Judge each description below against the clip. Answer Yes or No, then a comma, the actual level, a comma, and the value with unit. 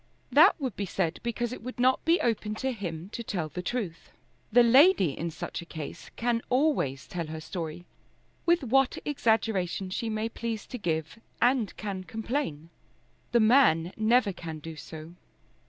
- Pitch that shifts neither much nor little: No, wide, 6.4 semitones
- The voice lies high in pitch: Yes, high, 215 Hz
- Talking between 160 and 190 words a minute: Yes, average, 170 wpm